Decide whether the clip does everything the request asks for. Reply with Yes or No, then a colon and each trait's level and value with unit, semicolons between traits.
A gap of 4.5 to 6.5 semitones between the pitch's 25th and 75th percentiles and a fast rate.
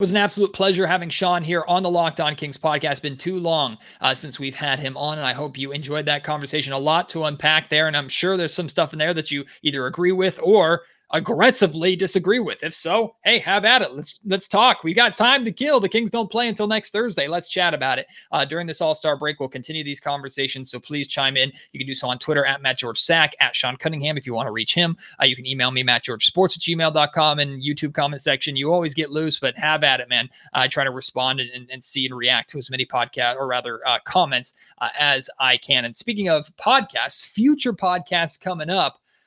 Yes: average, 5.0 semitones; fast, 250 wpm